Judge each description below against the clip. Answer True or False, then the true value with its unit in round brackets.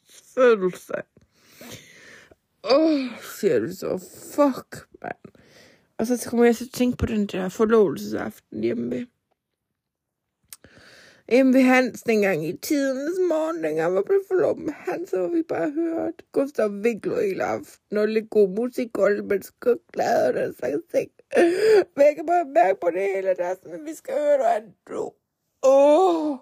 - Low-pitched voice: False (255 Hz)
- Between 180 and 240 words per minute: False (165 wpm)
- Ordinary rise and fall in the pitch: False (8.4 semitones)